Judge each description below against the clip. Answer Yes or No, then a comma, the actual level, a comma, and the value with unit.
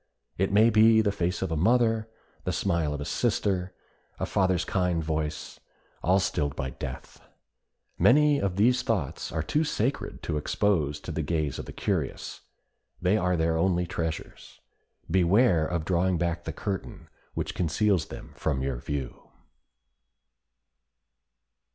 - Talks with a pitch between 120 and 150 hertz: No, very low, 90 Hz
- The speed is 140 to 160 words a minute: Yes, average, 145 wpm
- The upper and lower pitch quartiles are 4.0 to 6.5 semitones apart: Yes, average, 4.4 semitones